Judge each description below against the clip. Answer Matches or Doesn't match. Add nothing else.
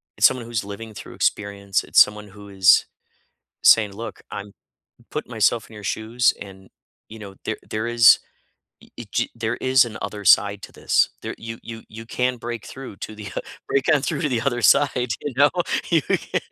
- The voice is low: Matches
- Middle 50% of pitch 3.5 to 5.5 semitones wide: Doesn't match